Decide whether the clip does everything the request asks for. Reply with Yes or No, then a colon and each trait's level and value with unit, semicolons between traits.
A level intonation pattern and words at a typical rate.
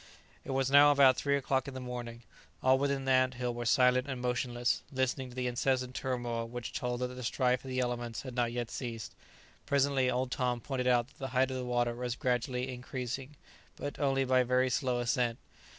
No: narrow, 1.4 semitones; fast, 210 wpm